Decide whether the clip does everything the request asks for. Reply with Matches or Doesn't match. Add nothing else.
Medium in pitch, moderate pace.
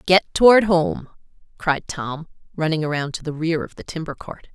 Matches